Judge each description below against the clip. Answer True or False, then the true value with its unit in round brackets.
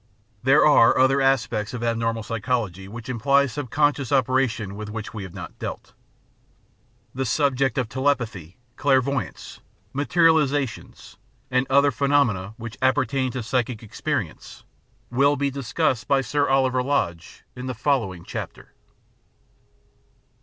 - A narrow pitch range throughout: False (3.7 semitones)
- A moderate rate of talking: False (130 wpm)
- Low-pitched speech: True (130 Hz)